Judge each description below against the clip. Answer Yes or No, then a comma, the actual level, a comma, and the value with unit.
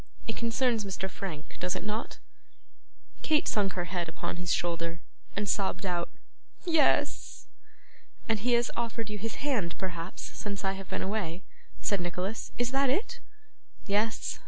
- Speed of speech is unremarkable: Yes, average, 155 wpm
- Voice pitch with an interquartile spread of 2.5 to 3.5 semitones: No, average, 4.2 semitones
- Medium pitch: No, high, 200 Hz